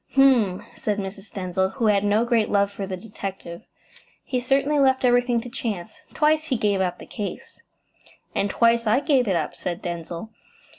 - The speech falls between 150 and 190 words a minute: Yes, average, 180 wpm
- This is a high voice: Yes, high, 215 Hz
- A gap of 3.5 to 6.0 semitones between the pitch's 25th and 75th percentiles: Yes, average, 4.5 semitones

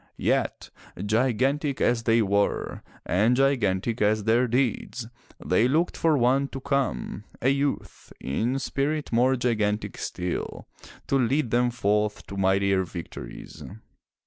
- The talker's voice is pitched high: No, low, 120 Hz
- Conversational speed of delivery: No, slow, 125 wpm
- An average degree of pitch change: Yes, average, 4.5 semitones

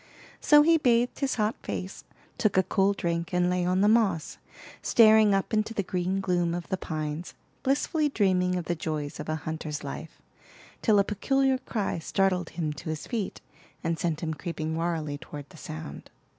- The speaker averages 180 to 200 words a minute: Yes, average, 185 wpm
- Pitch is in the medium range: Yes, medium, 180 Hz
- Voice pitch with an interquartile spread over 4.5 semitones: Yes, average, 4.9 semitones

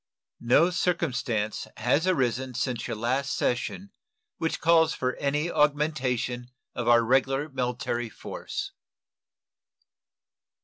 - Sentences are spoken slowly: Yes, slow, 100 wpm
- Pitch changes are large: No, average, 3.8 semitones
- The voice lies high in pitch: No, low, 130 Hz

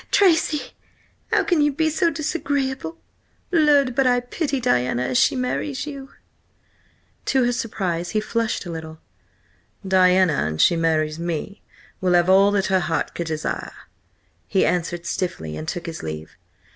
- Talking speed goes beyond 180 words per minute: No, average, 155 wpm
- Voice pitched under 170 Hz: No, high, 195 Hz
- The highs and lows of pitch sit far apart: Yes, wide, 8.8 semitones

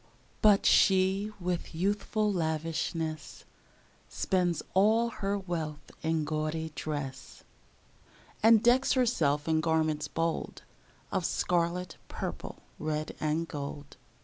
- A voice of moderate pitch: Yes, medium, 165 Hz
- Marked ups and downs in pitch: No, average, 4.0 semitones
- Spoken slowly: Yes, slow, 100 wpm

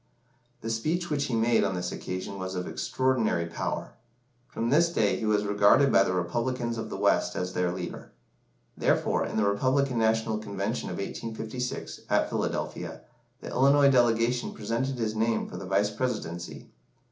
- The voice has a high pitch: No, low, 110 Hz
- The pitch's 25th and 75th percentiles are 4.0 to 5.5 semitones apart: Yes, average, 4.3 semitones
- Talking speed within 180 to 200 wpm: No, average, 165 wpm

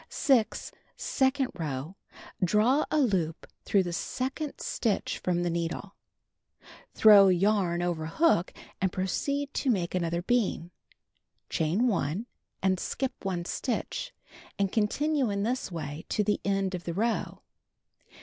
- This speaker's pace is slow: Yes, slow, 130 wpm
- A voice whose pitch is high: Yes, high, 195 Hz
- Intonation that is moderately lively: No, wide, 5.7 semitones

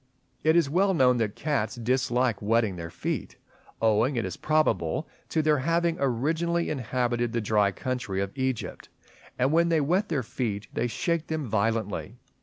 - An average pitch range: No, wide, 5.8 semitones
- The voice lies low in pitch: Yes, low, 125 Hz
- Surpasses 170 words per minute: No, average, 165 wpm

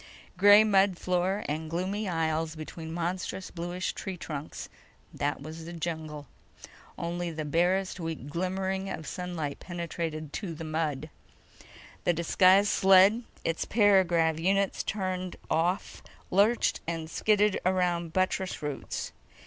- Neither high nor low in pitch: Yes, medium, 175 Hz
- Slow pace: Yes, slow, 115 wpm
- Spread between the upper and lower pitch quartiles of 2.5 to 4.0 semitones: Yes, average, 2.8 semitones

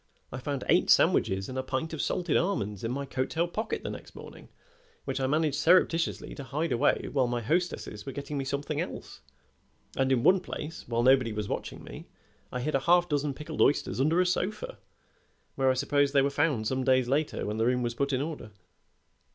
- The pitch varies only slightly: No, average, 3.6 semitones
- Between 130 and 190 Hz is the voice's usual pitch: Yes, medium, 140 Hz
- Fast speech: Yes, fast, 210 wpm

